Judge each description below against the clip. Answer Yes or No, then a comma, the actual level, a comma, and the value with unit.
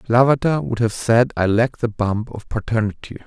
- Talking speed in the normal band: Yes, average, 185 wpm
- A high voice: No, low, 115 Hz